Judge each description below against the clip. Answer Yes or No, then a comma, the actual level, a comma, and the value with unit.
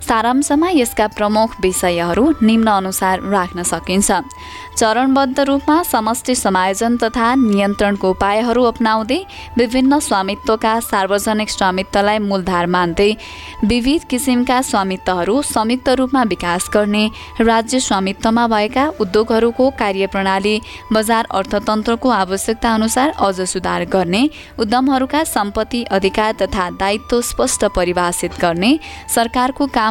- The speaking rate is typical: No, slow, 100 wpm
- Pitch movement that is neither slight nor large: Yes, average, 4.1 semitones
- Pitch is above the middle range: Yes, high, 220 Hz